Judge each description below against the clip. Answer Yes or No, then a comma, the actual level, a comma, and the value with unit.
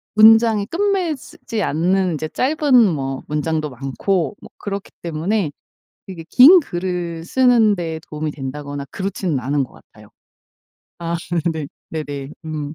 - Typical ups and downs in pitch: No, wide, 6.2 semitones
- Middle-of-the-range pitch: Yes, medium, 170 Hz